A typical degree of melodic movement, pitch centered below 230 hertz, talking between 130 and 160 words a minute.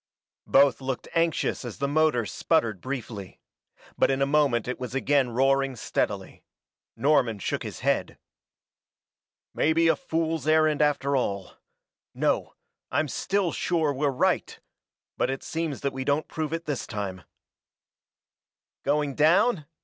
Yes: average, 3.4 semitones; medium, 140 Hz; slow, 135 wpm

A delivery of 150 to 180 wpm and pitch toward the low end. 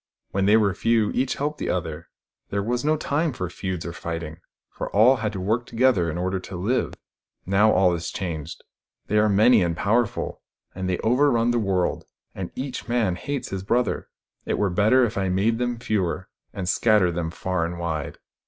No: average, 200 wpm; low, 100 Hz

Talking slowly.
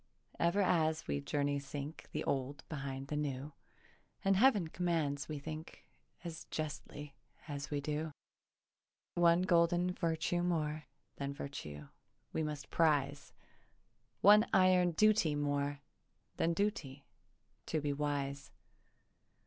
Yes: slow, 115 wpm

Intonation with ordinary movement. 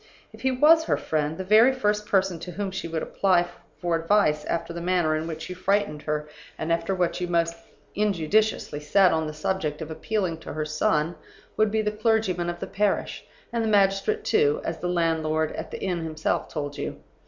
Yes: average, 4.6 semitones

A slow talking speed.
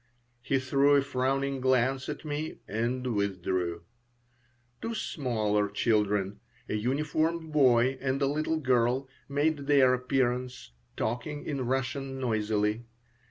Yes: slow, 115 wpm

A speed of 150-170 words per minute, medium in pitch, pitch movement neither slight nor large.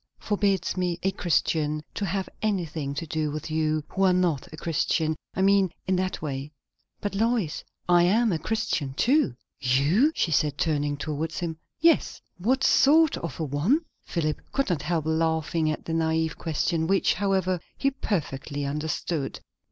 Yes: average, 165 wpm; medium, 165 Hz; average, 4.0 semitones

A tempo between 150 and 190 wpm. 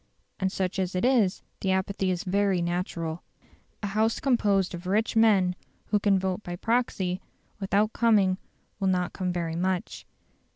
Yes: average, 160 wpm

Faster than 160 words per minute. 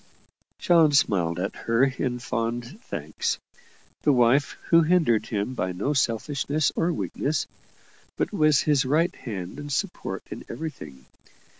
No: slow, 135 wpm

